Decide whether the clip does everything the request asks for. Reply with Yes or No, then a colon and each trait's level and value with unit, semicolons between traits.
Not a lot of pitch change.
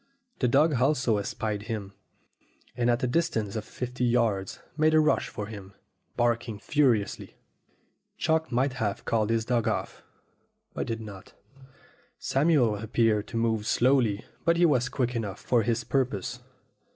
No: average, 3.2 semitones